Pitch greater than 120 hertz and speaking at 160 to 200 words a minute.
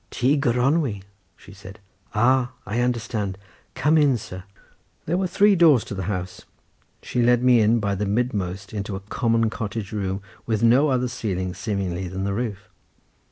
No: low, 110 Hz; average, 165 wpm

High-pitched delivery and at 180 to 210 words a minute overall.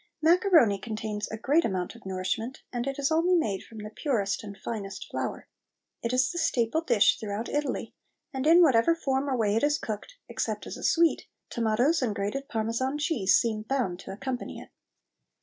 Yes: high, 240 Hz; average, 185 wpm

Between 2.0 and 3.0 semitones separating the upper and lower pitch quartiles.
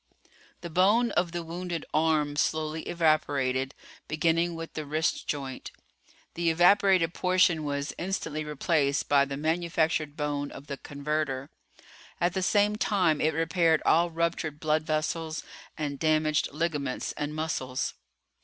Yes: narrow, 2.5 semitones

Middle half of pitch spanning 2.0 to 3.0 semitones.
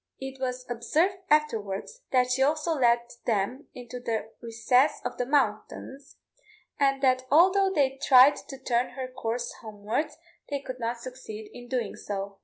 Yes: average, 2.7 semitones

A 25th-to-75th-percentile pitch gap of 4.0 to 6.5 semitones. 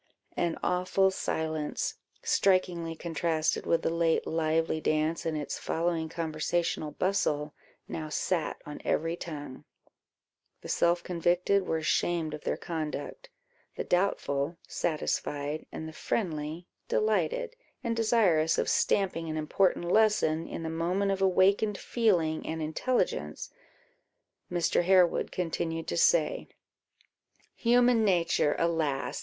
No: average, 3.1 semitones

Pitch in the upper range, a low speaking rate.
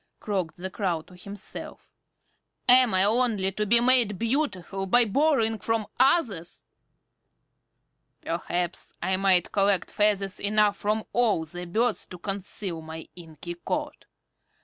Yes: high, 200 Hz; slow, 125 wpm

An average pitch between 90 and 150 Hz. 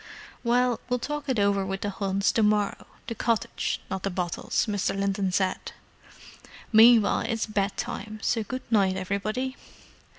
No: high, 210 Hz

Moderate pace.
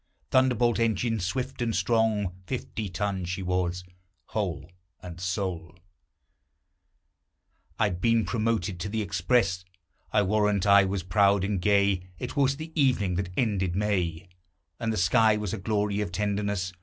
Yes: average, 145 wpm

